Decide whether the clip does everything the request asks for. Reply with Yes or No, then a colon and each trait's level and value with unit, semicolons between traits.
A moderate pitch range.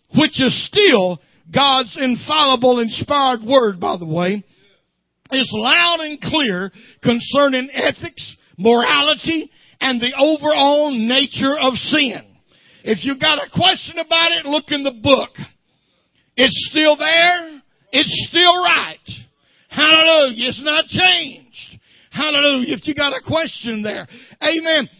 Yes: average, 3.7 semitones